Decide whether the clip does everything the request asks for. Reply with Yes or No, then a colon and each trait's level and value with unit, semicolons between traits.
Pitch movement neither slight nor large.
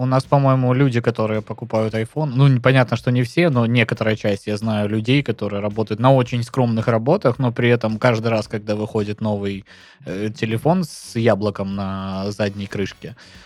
Yes: average, 3.1 semitones